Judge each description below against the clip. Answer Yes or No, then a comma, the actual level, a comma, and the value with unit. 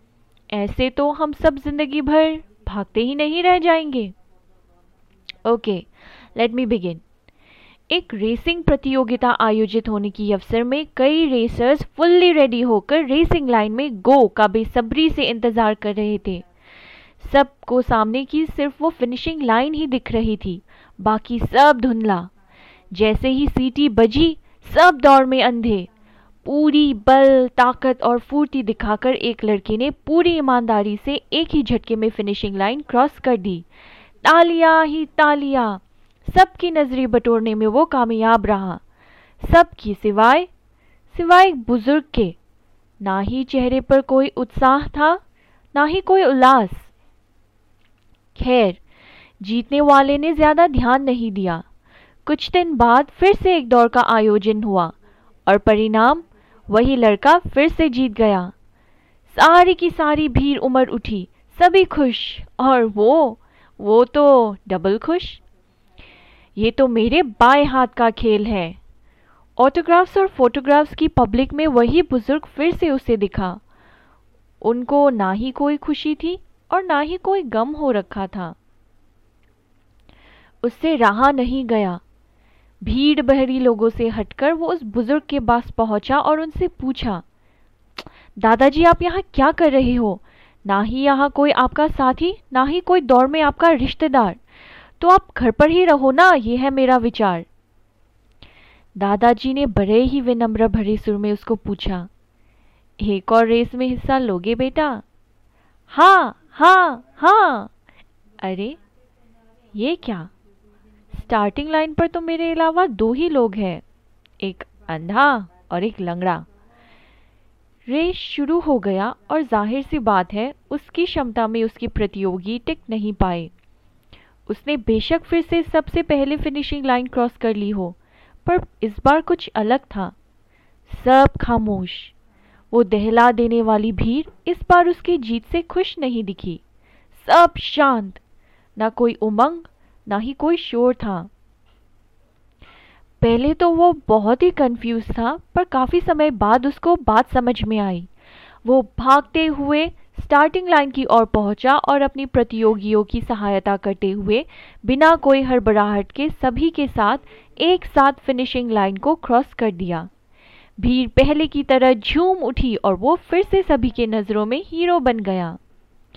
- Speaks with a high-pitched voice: Yes, high, 245 Hz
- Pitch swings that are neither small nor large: No, wide, 6.2 semitones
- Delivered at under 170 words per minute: Yes, average, 140 wpm